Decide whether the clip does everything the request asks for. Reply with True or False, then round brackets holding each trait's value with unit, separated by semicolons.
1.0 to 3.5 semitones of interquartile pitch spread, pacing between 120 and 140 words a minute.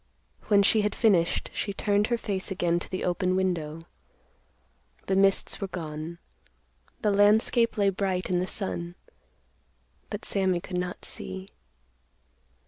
True (2.4 semitones; 135 wpm)